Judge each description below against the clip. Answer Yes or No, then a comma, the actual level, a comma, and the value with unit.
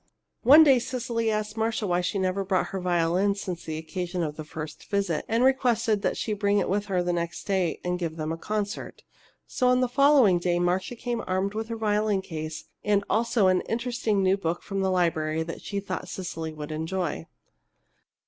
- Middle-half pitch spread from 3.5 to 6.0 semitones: Yes, average, 4.1 semitones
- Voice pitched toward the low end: No, high, 195 Hz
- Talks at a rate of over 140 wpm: Yes, average, 200 wpm